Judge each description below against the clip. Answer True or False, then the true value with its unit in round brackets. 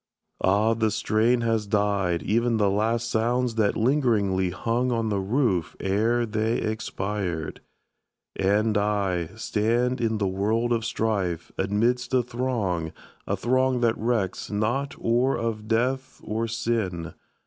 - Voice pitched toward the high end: False (110 Hz)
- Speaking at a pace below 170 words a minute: True (135 wpm)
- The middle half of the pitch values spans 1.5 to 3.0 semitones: True (2.7 semitones)